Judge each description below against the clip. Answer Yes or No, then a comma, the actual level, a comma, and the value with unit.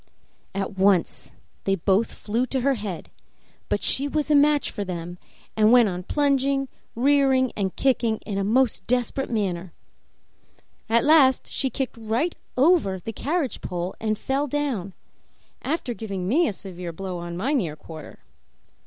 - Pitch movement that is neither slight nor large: No, wide, 6.1 semitones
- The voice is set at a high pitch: Yes, high, 230 Hz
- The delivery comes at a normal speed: Yes, average, 155 wpm